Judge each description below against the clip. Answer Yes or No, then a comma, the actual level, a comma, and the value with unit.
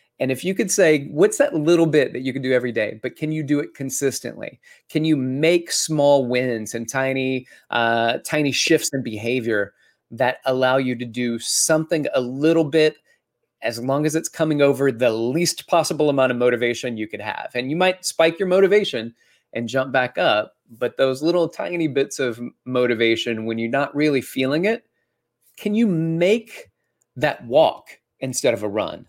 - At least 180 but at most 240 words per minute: Yes, average, 185 wpm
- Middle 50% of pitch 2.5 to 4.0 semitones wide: No, average, 4.5 semitones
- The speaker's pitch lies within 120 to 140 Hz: Yes, low, 135 Hz